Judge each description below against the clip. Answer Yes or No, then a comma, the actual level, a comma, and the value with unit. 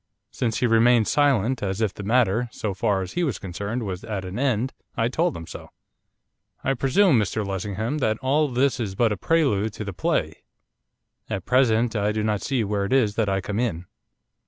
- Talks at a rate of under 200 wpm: No, fast, 205 wpm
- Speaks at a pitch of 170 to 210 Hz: No, low, 110 Hz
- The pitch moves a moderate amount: Yes, average, 4.0 semitones